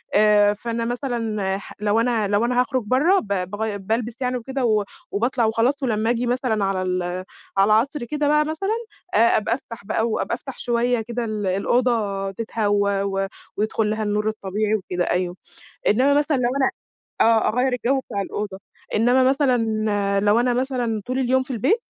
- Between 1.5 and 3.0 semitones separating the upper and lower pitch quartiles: No, average, 3.5 semitones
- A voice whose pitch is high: Yes, high, 230 Hz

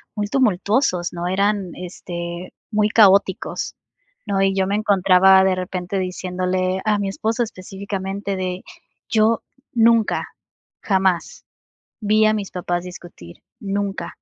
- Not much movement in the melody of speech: Yes, narrow, 2.2 semitones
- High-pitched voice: Yes, high, 195 Hz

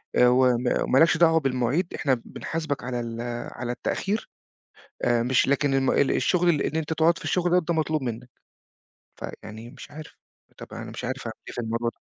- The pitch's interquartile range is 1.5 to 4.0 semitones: No, average, 4.8 semitones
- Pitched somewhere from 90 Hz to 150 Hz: Yes, low, 135 Hz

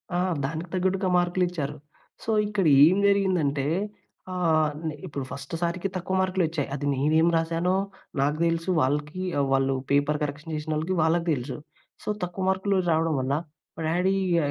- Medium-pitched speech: Yes, medium, 165 Hz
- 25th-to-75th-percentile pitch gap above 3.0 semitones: Yes, average, 3.7 semitones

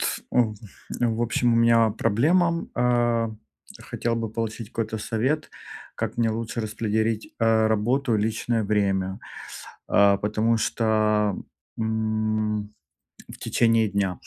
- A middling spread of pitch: No, narrow, 1.5 semitones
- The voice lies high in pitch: No, low, 110 Hz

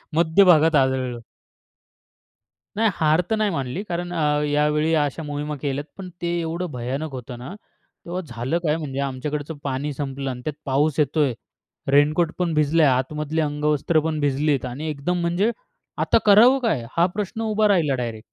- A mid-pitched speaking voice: Yes, medium, 150 Hz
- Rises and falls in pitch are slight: No, average, 3.6 semitones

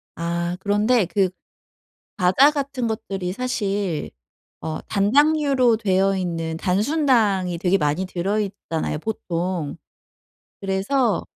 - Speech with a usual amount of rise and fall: Yes, average, 4.4 semitones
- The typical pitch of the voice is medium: No, high, 195 Hz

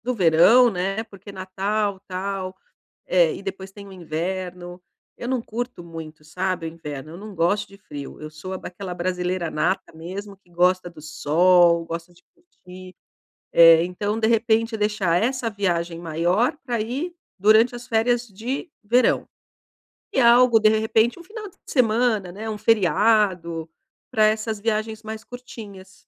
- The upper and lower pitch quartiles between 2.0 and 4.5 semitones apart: Yes, average, 4.0 semitones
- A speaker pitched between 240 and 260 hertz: No, high, 195 Hz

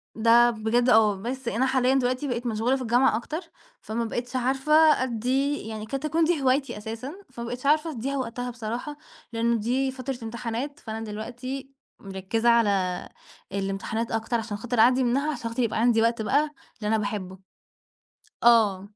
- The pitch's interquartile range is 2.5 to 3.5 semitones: Yes, average, 2.9 semitones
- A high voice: Yes, high, 240 Hz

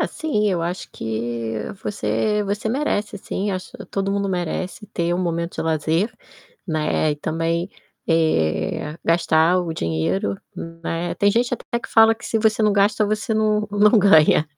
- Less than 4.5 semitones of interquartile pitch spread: No, average, 4.9 semitones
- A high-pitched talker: No, medium, 180 Hz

